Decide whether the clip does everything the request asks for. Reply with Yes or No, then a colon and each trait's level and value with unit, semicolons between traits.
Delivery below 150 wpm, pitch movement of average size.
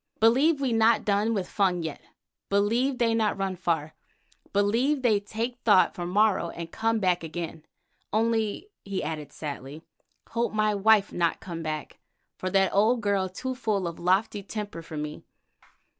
No: average, 160 wpm; average, 4.4 semitones